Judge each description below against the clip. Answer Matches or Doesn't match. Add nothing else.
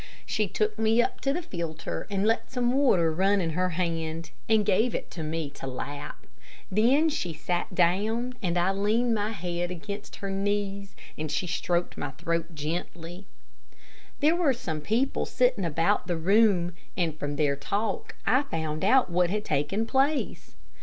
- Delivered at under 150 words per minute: Doesn't match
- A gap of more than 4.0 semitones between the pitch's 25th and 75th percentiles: Matches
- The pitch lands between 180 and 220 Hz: Matches